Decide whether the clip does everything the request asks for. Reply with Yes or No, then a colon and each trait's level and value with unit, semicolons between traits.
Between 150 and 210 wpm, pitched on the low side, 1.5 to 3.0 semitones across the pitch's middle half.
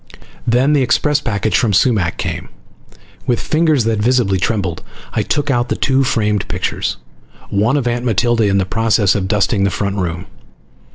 No: average, 170 wpm; low, 115 Hz; average, 4.1 semitones